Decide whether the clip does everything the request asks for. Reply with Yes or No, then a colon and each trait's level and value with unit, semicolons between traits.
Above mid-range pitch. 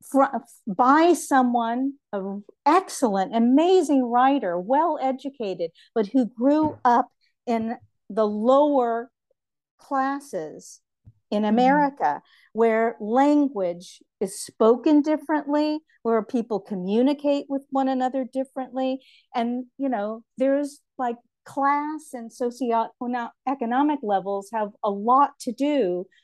Yes: very high, 255 Hz